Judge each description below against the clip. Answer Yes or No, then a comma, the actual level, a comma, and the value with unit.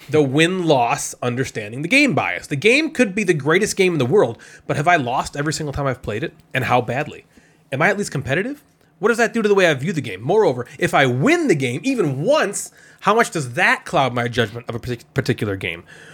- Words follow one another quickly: Yes, fast, 240 wpm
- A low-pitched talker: No, medium, 155 Hz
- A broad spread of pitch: Yes, wide, 7.4 semitones